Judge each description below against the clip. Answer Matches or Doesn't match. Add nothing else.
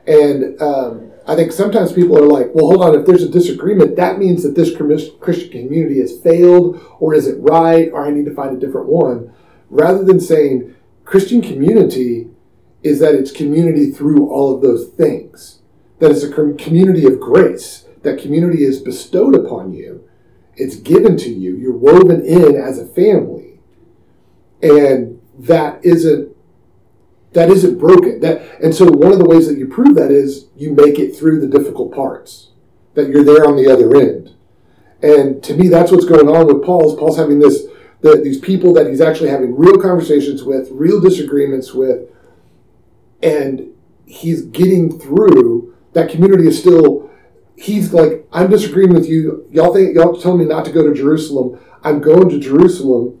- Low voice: Doesn't match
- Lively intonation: Doesn't match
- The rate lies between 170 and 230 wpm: Matches